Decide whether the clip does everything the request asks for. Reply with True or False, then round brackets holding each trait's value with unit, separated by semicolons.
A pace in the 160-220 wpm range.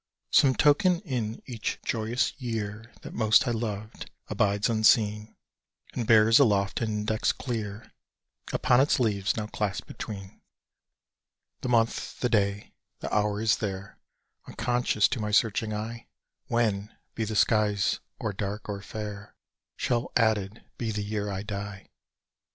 False (140 wpm)